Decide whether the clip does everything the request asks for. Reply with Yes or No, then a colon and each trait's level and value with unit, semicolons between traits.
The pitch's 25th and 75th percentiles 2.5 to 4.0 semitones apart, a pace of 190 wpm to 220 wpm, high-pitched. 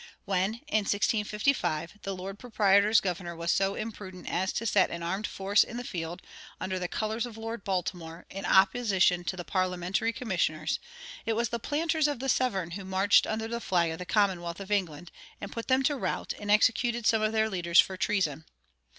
Yes: average, 3.7 semitones; average, 195 wpm; high, 195 Hz